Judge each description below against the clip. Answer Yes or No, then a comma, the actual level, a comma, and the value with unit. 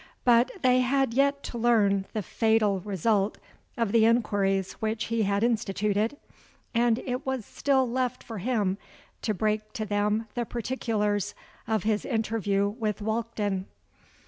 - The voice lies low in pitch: No, high, 220 Hz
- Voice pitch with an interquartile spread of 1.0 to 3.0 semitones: Yes, narrow, 2.6 semitones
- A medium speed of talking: Yes, average, 145 wpm